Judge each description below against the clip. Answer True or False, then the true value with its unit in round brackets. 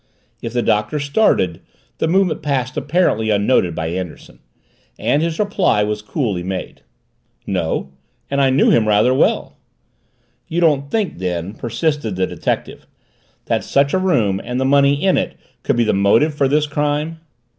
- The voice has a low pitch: True (130 Hz)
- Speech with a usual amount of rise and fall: False (6.3 semitones)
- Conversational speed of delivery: True (160 wpm)